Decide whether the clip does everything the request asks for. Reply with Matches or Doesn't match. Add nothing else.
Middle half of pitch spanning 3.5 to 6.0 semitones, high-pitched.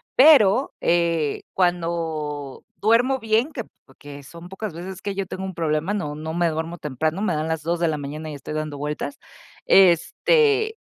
Doesn't match